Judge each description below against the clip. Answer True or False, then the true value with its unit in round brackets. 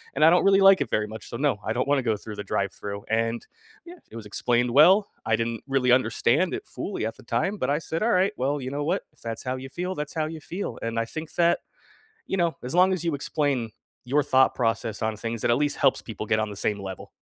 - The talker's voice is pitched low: True (130 Hz)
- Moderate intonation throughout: False (6.1 semitones)